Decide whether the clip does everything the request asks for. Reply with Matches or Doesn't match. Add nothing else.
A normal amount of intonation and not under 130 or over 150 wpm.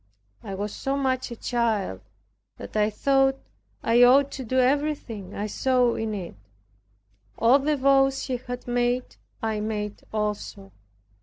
Matches